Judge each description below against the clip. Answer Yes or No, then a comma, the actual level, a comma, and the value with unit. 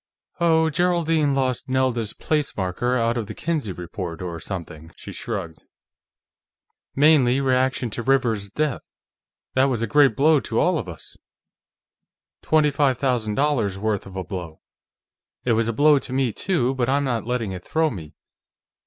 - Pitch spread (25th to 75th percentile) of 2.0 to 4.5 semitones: No, wide, 5.5 semitones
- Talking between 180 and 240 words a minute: No, average, 160 wpm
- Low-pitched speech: Yes, low, 125 Hz